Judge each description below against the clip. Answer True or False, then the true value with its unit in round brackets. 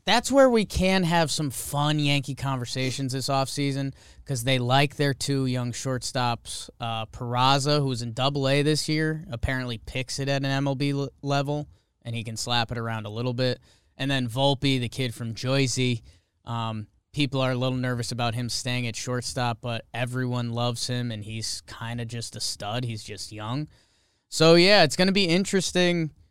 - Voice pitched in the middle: False (130 Hz)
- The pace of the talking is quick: False (185 wpm)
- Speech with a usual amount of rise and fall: True (3.1 semitones)